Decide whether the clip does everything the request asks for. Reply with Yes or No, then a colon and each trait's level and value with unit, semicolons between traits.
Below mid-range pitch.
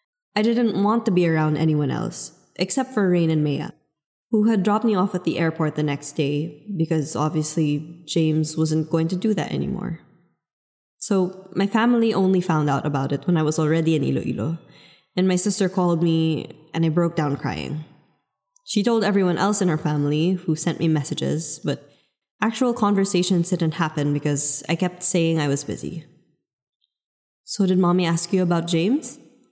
No: medium, 170 Hz